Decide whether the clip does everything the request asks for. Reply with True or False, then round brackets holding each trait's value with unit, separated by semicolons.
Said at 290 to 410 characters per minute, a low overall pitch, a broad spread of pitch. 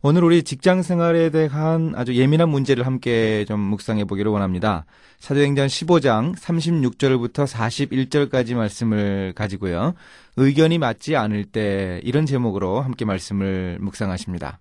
True (310 characters per minute; 125 Hz; 6.3 semitones)